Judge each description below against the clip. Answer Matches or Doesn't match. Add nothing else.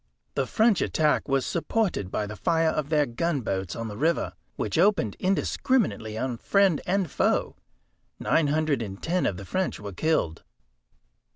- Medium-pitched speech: Matches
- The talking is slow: Doesn't match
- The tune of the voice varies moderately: Doesn't match